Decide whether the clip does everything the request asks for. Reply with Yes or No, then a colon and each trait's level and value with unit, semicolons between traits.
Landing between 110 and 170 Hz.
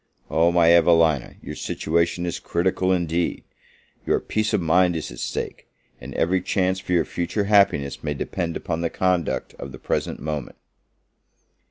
No: very low, 85 Hz